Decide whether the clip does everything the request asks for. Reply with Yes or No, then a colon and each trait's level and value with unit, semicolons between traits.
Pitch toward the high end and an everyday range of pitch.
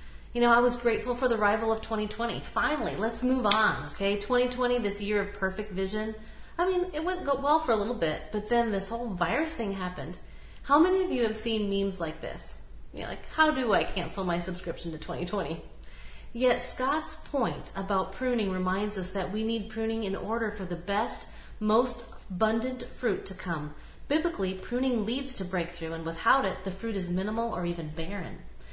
Yes: high, 215 Hz; average, 4.0 semitones